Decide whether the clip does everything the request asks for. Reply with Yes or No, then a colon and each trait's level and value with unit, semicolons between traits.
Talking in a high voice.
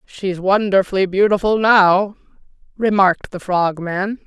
Yes: high, 195 Hz